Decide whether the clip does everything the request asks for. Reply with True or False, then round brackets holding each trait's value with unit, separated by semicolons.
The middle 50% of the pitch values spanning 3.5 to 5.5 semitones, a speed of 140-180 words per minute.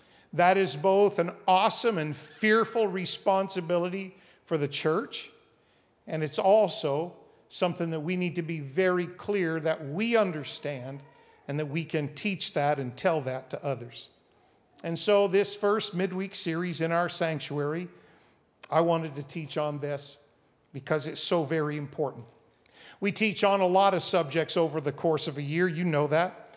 True (4.2 semitones; 165 wpm)